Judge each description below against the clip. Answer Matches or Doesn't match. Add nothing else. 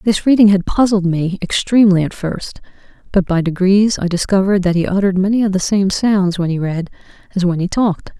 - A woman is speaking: Matches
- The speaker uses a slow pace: Doesn't match